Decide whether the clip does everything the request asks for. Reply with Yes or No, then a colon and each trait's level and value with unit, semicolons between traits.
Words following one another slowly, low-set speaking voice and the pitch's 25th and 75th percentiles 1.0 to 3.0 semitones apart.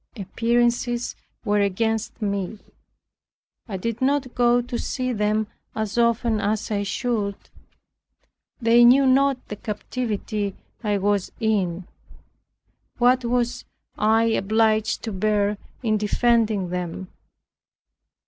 No: slow, 110 wpm; high, 220 Hz; average, 2.7 semitones